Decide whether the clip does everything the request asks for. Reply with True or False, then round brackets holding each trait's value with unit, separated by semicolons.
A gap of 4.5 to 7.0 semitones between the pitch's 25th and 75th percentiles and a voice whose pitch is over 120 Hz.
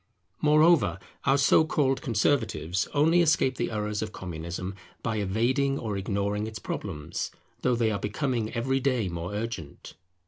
False (5.2 semitones; 115 Hz)